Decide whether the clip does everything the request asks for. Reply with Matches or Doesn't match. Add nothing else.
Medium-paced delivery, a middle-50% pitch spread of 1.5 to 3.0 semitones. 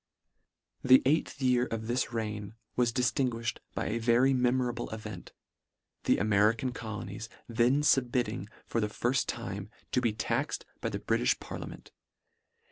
Matches